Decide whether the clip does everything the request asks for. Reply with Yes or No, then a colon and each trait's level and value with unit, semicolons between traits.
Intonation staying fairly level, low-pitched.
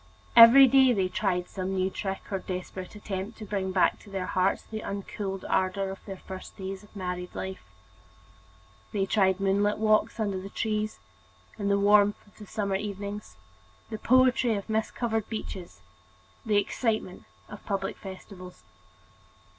No: narrow, 2.1 semitones; high, 200 Hz